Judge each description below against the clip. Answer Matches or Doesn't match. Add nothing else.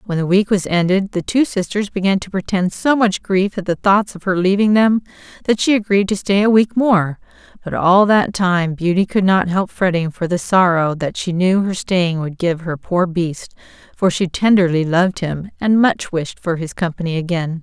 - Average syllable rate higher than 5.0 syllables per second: Doesn't match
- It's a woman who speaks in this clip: Matches